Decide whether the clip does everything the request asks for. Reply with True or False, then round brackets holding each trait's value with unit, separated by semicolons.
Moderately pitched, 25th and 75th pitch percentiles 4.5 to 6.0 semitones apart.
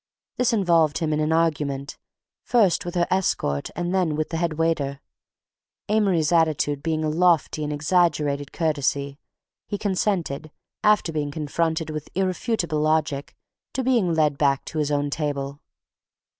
False (155 Hz; 3.1 semitones)